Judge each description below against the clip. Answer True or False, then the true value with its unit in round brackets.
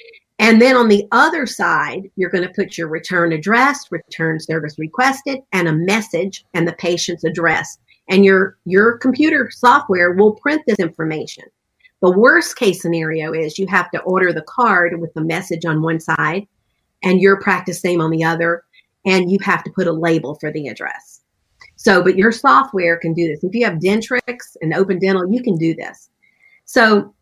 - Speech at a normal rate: True (185 wpm)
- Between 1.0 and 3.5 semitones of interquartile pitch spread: False (4.3 semitones)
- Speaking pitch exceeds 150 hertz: True (185 Hz)